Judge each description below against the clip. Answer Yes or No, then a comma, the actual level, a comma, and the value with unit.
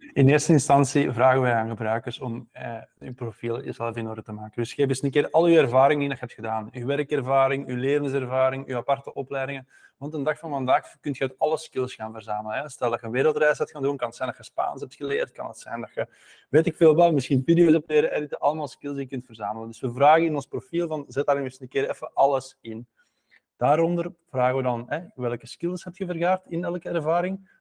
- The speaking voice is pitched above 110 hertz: Yes, low, 135 Hz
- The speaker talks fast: Yes, fast, 245 wpm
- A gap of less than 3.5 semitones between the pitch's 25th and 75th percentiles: No, average, 3.9 semitones